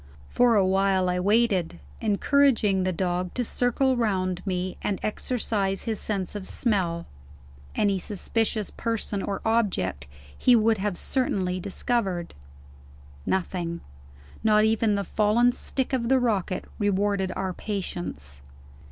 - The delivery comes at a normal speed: No, slow, 125 wpm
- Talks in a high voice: Yes, high, 200 Hz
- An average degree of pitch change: Yes, average, 3.4 semitones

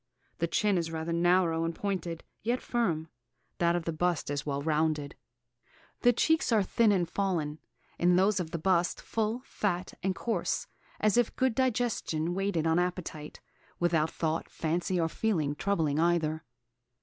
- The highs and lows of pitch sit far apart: No, average, 3.8 semitones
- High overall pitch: No, medium, 175 Hz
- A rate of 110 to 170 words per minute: Yes, average, 155 wpm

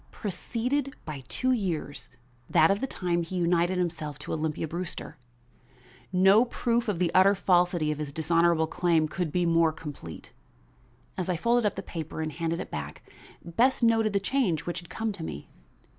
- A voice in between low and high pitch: Yes, medium, 175 Hz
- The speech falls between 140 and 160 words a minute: No, average, 175 wpm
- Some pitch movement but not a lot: Yes, average, 3.9 semitones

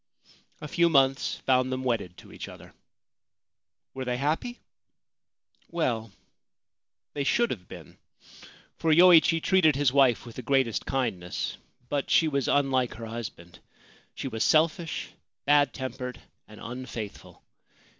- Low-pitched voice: Yes, low, 130 Hz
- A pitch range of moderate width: Yes, average, 4.3 semitones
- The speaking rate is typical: No, slow, 130 wpm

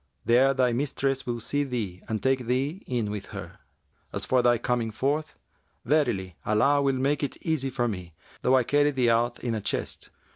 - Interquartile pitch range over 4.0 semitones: No, average, 3.0 semitones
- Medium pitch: No, low, 125 Hz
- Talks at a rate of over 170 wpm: Yes, average, 190 wpm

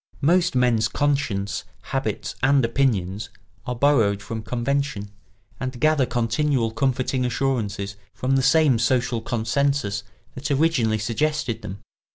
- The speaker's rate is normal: No, slow, 120 wpm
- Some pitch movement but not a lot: Yes, average, 3.9 semitones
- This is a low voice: Yes, low, 125 Hz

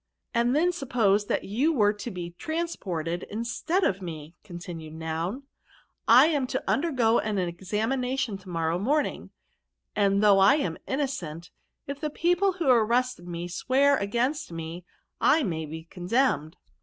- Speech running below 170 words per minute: Yes, average, 155 wpm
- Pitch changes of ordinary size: No, wide, 7.6 semitones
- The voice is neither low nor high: No, high, 210 Hz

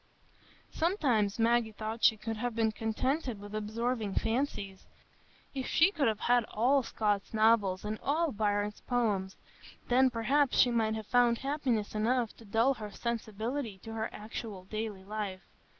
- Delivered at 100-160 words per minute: Yes, average, 150 wpm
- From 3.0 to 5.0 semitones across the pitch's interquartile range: No, narrow, 2.6 semitones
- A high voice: Yes, high, 225 Hz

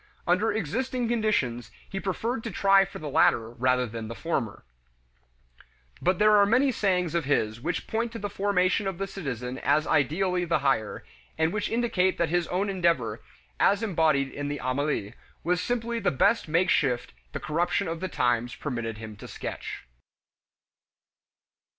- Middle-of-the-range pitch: Yes, medium, 170 Hz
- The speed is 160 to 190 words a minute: Yes, average, 165 wpm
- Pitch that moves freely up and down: Yes, wide, 7.4 semitones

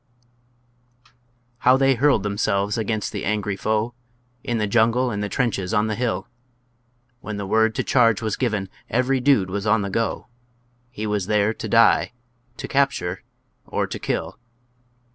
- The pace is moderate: Yes, average, 160 wpm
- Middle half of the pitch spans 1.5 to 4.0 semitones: Yes, average, 2.8 semitones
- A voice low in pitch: Yes, low, 110 Hz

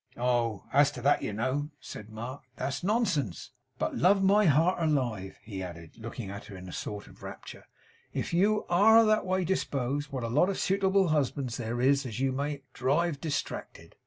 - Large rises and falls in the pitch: Yes, wide, 7.0 semitones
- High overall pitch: No, medium, 140 Hz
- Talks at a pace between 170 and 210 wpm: Yes, average, 190 wpm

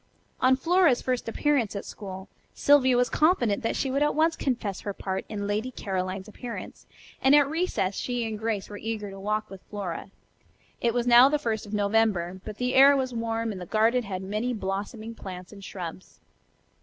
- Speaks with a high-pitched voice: Yes, high, 225 Hz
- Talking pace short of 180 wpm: No, average, 195 wpm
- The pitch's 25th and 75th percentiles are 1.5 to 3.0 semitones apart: No, average, 4.1 semitones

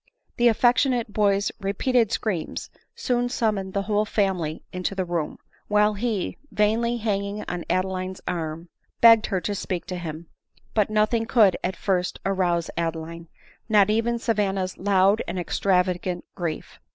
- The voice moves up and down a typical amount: Yes, average, 3.1 semitones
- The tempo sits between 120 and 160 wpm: Yes, average, 150 wpm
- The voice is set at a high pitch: Yes, high, 195 Hz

